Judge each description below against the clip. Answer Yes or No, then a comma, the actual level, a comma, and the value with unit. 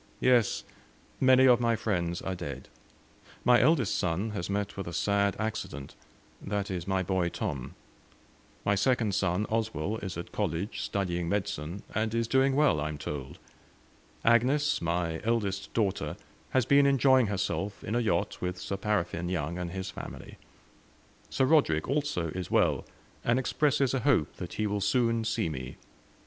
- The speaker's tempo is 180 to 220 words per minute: No, average, 160 wpm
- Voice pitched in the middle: No, low, 100 Hz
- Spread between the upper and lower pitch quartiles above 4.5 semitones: Yes, average, 5.0 semitones